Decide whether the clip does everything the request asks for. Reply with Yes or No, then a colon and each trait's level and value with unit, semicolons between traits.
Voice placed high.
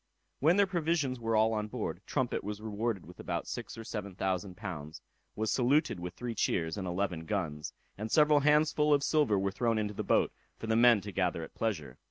No: low, 110 Hz